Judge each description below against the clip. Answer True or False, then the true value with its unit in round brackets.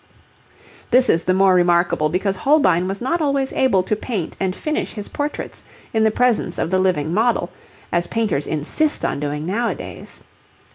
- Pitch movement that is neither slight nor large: False (5.9 semitones)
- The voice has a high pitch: True (195 Hz)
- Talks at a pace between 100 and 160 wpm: False (170 wpm)